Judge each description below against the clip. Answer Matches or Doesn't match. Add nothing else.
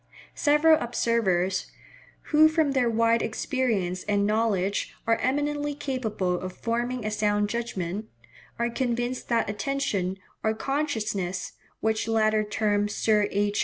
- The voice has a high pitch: Matches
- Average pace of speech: Doesn't match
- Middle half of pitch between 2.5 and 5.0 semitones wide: Matches